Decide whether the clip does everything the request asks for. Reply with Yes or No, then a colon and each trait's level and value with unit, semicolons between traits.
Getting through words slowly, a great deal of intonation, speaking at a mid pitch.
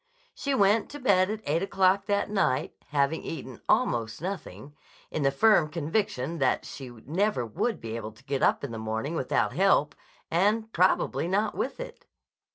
No: average, 170 wpm; wide, 7.5 semitones; medium, 165 Hz